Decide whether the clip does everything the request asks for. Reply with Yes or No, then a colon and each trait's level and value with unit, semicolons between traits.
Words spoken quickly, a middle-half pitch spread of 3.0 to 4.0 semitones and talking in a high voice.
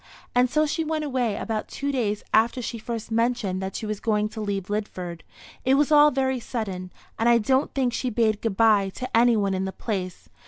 Yes: fast, 220 wpm; average, 3.7 semitones; high, 225 Hz